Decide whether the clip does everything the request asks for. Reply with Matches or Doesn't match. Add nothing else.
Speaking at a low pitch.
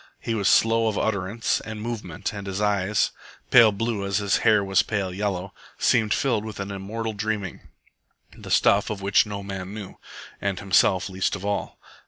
Matches